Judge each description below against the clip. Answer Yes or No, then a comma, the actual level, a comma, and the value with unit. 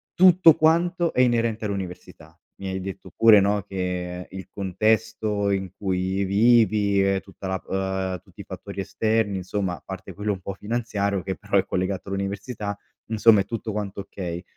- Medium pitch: No, low, 100 Hz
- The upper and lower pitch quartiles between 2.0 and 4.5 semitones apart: Yes, narrow, 2.5 semitones